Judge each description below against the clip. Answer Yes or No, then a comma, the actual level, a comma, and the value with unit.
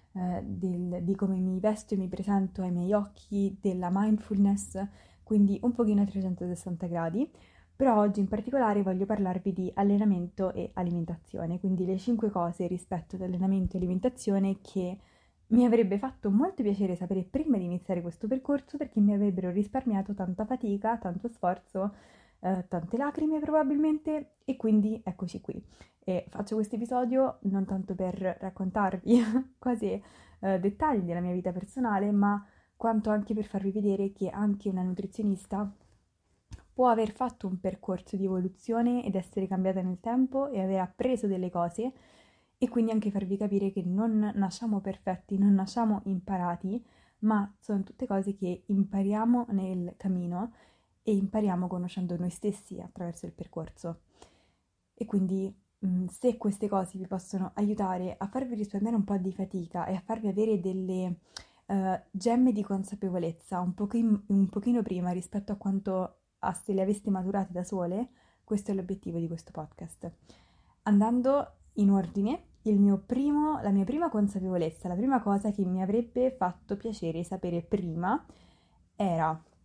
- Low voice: No, high, 195 Hz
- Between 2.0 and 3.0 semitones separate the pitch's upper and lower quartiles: Yes, average, 2.7 semitones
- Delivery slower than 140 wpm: No, average, 150 wpm